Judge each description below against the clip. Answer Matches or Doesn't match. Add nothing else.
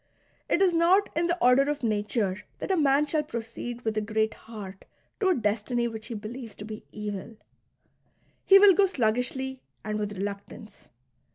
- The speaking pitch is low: Doesn't match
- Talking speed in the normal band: Matches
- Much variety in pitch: Matches